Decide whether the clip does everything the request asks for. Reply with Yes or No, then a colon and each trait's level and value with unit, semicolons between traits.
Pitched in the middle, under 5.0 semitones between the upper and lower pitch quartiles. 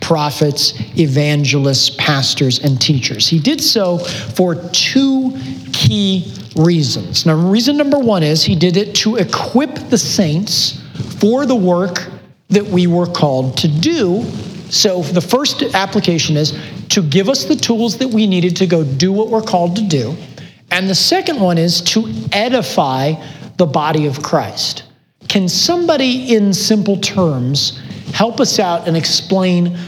No: medium, 175 Hz; average, 5.3 semitones